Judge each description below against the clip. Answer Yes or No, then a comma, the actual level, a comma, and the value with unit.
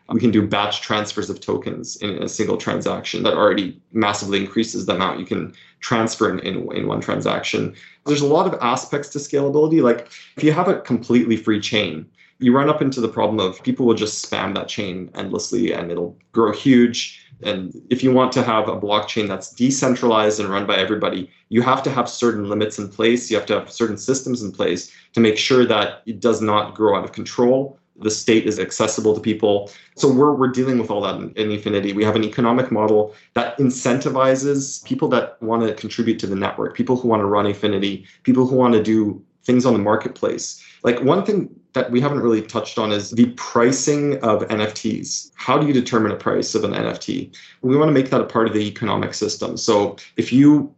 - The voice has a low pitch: Yes, low, 115 Hz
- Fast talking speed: Yes, fast, 215 wpm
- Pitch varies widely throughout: No, average, 3.4 semitones